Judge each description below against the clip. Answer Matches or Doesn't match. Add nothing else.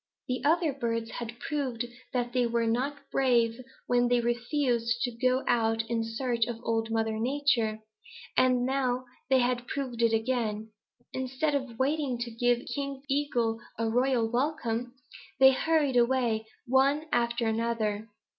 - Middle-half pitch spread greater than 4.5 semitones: Doesn't match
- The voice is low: Doesn't match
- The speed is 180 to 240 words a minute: Doesn't match